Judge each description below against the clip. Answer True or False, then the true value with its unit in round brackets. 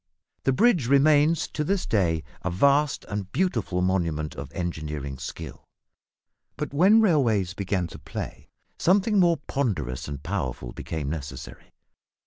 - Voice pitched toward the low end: True (100 Hz)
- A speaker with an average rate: False (130 wpm)